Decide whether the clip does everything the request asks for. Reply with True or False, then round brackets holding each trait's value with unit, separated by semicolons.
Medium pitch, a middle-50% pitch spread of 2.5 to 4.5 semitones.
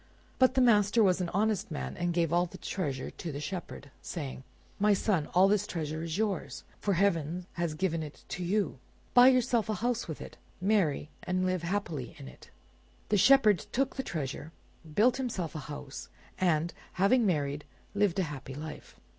False (180 Hz; 5.2 semitones)